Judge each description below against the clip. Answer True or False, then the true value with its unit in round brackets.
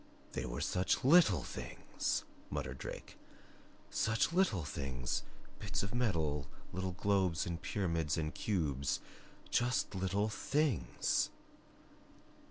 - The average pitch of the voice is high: False (95 Hz)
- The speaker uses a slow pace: True (105 wpm)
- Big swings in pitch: True (5.8 semitones)